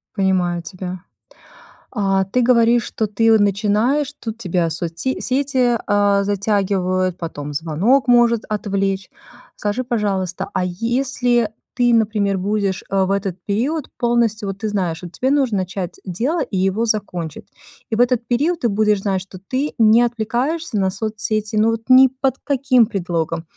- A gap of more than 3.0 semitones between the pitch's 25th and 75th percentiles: Yes, average, 4.0 semitones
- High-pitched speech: Yes, high, 210 Hz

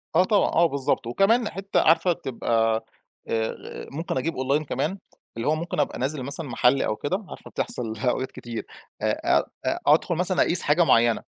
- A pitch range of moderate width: No, wide, 5.8 semitones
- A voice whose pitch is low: No, medium, 145 Hz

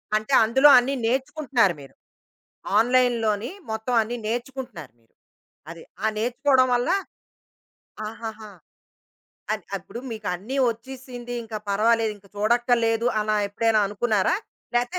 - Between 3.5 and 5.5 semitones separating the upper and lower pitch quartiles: No, narrow, 2.5 semitones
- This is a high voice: Yes, high, 230 Hz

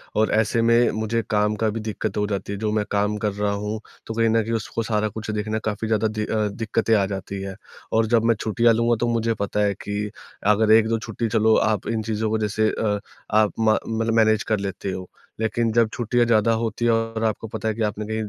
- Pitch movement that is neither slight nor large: No, narrow, 1.3 semitones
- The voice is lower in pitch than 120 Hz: Yes, low, 110 Hz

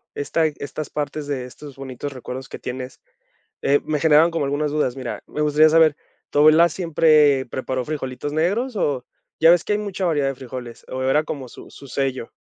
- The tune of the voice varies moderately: Yes, average, 3.0 semitones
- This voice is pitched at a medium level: Yes, medium, 145 Hz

